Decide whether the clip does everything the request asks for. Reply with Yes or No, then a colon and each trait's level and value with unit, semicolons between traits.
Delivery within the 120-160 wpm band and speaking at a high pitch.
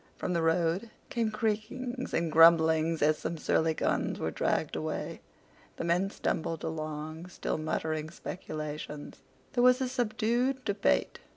No: slow, 135 wpm; medium, 170 Hz